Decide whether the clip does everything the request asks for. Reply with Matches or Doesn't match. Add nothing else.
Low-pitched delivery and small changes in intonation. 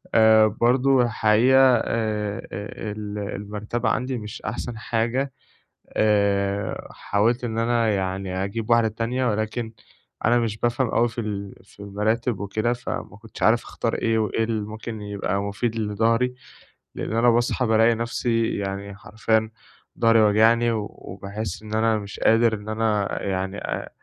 Matches